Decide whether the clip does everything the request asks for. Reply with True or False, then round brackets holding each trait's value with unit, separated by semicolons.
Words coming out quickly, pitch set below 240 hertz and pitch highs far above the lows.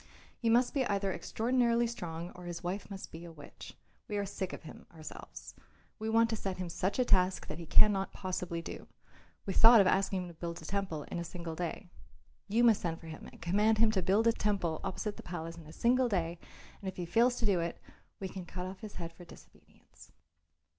False (230 wpm; 190 Hz; 4.1 semitones)